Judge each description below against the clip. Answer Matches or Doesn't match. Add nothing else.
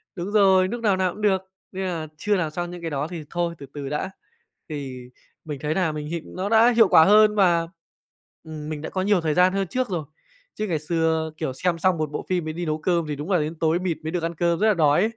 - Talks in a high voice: Doesn't match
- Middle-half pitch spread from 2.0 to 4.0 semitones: Matches